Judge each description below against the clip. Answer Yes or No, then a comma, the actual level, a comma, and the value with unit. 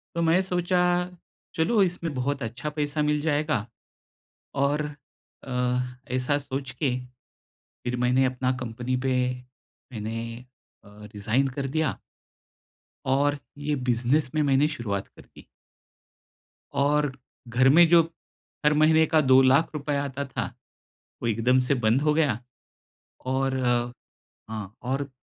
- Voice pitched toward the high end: No, medium, 140 Hz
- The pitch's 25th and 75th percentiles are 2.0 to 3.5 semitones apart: Yes, average, 3.2 semitones